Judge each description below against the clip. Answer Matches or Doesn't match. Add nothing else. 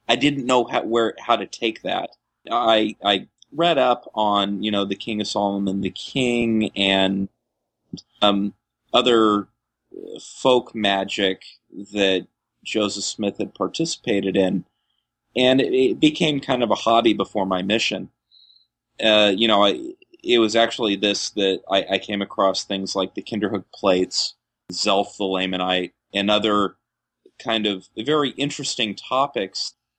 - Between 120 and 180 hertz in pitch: Doesn't match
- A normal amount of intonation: Matches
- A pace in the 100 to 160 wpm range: Matches